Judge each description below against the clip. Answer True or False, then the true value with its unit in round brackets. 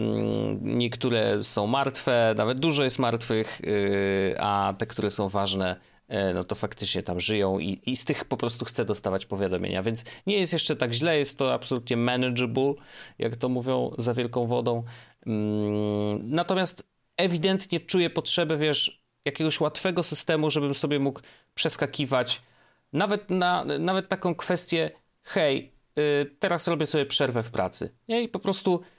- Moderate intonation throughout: False (6.4 semitones)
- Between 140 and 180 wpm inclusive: True (145 wpm)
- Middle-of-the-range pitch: False (130 Hz)